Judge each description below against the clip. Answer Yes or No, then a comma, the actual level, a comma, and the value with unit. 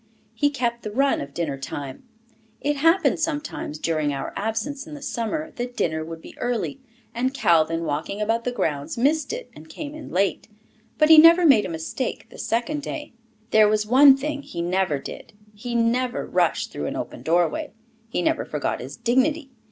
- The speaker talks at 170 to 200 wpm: Yes, average, 185 wpm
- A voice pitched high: Yes, high, 235 Hz